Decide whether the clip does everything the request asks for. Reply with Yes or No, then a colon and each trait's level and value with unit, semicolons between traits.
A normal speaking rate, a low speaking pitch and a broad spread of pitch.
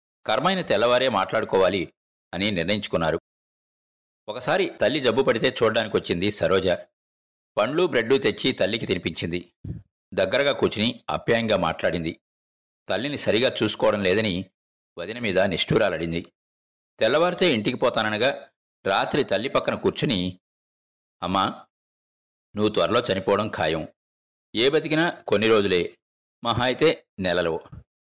Yes: average, 100 wpm; very low, 85 Hz; wide, 7.6 semitones